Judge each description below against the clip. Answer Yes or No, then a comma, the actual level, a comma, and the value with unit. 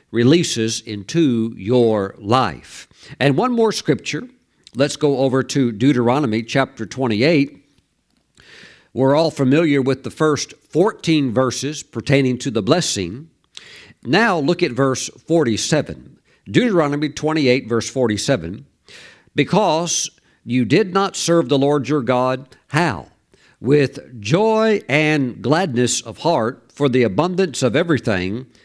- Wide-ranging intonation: No, average, 3.9 semitones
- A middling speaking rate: No, slow, 120 wpm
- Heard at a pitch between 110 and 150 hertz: Yes, low, 135 Hz